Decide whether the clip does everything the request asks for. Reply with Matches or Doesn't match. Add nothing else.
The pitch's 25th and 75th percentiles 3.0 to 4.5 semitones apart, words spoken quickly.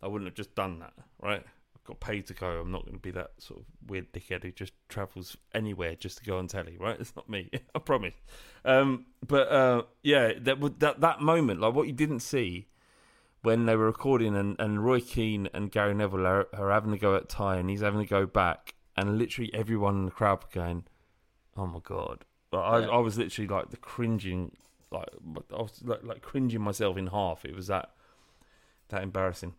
Matches